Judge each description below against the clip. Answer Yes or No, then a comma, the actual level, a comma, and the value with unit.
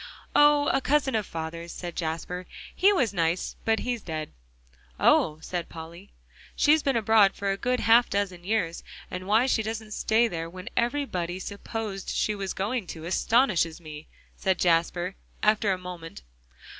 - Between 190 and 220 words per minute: No, average, 160 wpm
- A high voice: Yes, high, 195 Hz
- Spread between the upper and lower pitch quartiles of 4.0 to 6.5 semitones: Yes, average, 4.7 semitones